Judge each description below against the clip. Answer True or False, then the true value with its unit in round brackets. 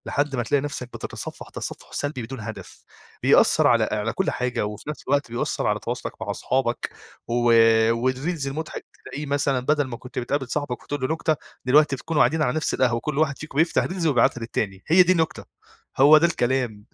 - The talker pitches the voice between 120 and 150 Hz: True (135 Hz)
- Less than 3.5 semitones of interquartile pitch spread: False (3.8 semitones)